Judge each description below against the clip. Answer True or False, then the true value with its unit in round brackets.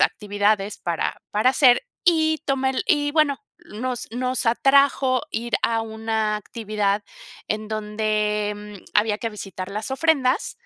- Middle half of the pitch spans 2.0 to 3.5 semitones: False (3.9 semitones)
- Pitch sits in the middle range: False (225 Hz)